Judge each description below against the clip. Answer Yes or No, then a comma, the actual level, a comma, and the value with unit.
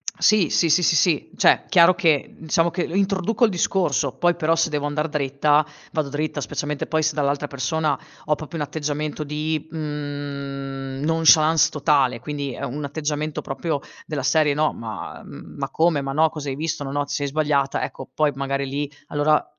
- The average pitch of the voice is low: No, medium, 150 Hz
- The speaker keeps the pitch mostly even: Yes, narrow, 2.1 semitones